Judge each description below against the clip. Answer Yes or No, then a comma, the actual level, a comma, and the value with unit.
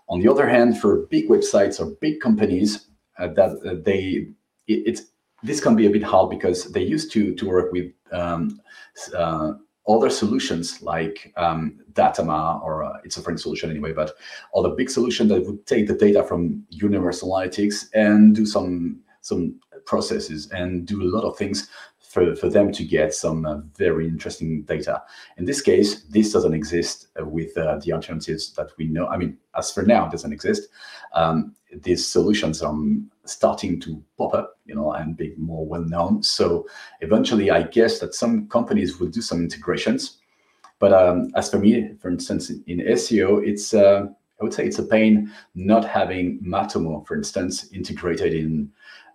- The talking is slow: No, average, 180 wpm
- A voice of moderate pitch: No, very low, 95 Hz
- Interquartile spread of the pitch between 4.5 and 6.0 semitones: Yes, average, 4.8 semitones